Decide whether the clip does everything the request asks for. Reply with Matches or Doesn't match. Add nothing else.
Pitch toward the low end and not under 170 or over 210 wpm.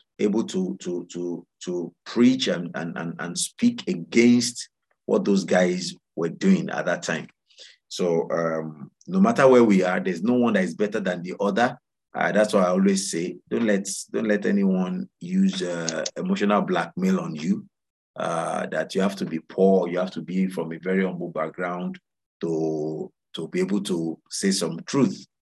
Matches